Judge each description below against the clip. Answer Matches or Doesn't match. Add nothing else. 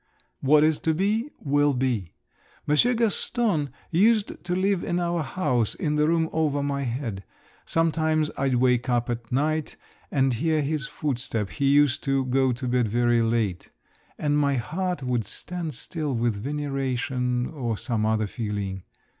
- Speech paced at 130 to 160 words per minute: Matches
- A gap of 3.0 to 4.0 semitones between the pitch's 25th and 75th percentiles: Doesn't match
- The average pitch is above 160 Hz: Doesn't match